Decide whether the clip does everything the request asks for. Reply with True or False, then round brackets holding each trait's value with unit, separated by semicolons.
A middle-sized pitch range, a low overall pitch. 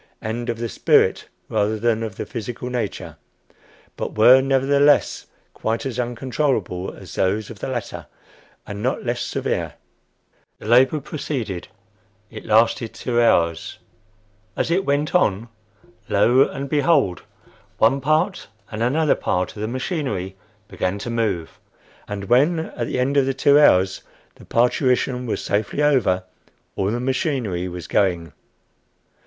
True (4.6 semitones; 120 Hz)